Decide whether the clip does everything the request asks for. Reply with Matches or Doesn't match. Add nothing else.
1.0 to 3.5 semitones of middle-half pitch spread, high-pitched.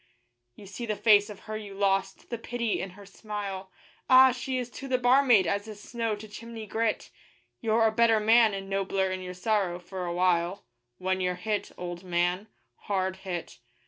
Matches